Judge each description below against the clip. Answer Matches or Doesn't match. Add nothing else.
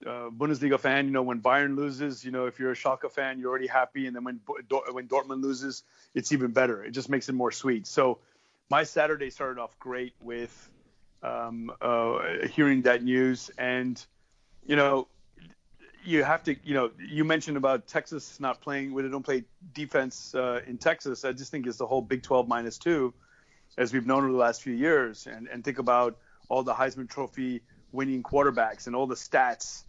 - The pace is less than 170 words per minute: Doesn't match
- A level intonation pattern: Matches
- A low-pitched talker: Matches